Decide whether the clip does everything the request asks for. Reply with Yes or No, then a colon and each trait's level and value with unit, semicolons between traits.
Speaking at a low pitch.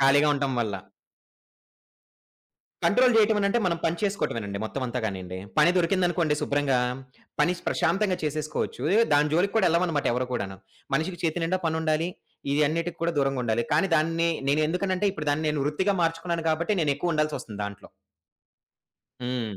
No: medium, 155 Hz